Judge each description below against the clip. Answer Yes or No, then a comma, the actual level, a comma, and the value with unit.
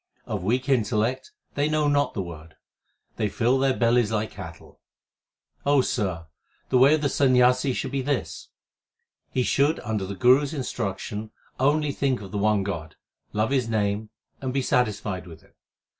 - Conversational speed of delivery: Yes, average, 165 wpm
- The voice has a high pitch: No, low, 120 Hz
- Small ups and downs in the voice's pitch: No, average, 4.7 semitones